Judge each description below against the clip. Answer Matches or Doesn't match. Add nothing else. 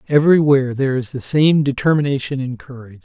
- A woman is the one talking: Doesn't match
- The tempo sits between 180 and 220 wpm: Doesn't match